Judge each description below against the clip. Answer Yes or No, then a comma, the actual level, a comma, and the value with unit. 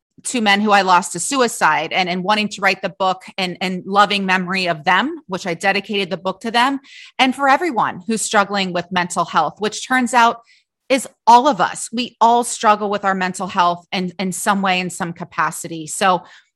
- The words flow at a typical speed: No, fast, 210 wpm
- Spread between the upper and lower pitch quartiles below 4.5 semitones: Yes, average, 3.7 semitones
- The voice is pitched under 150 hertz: No, high, 195 Hz